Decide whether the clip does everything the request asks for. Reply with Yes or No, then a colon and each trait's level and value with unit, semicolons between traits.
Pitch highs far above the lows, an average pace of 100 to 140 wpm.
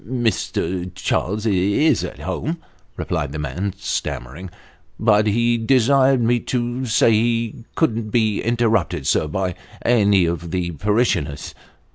No: average, 4.4 semitones; slow, 135 wpm